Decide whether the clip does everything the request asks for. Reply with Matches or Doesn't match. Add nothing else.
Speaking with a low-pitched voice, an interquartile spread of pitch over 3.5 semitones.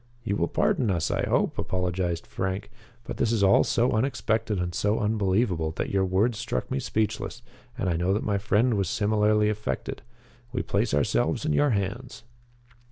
Doesn't match